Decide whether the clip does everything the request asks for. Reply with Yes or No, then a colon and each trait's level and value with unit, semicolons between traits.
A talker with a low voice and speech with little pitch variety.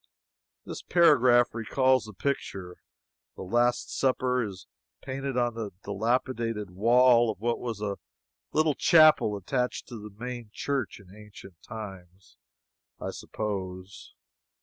No: low, 115 Hz; average, 3.9 semitones